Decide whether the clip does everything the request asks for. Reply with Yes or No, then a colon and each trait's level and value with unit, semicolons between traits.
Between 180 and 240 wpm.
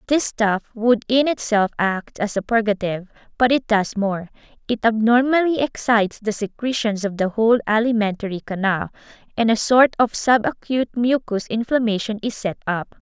No: average, 155 wpm